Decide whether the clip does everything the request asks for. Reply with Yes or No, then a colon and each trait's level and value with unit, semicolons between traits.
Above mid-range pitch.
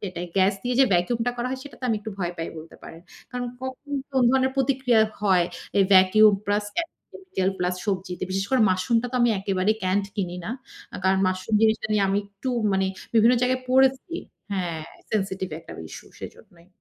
Yes: high, 205 Hz